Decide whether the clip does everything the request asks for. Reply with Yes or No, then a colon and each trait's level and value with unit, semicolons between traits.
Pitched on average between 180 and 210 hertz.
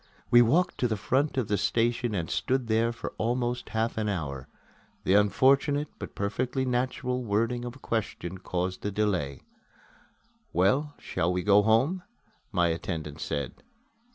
No: low, 110 Hz